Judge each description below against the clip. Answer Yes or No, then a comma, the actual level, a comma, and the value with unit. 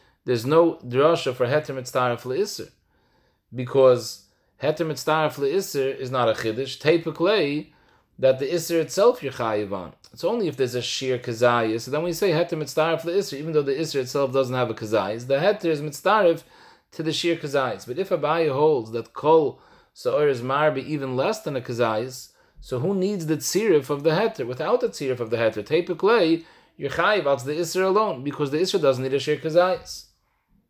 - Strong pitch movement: No, average, 4.6 semitones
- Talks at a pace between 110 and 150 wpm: No, average, 185 wpm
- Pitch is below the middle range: No, medium, 145 Hz